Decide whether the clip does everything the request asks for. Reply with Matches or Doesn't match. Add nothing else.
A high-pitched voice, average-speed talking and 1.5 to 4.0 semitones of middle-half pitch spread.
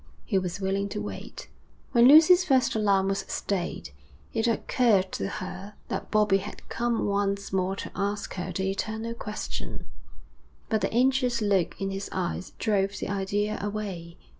Matches